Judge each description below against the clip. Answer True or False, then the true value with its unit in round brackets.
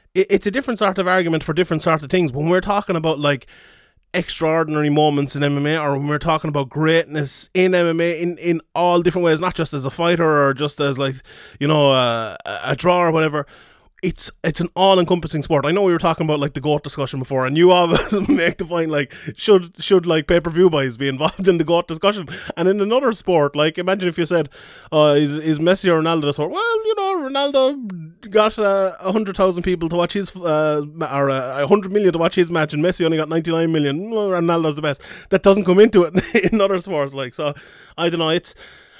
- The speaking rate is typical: False (225 wpm)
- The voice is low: False (170 Hz)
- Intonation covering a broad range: False (3.8 semitones)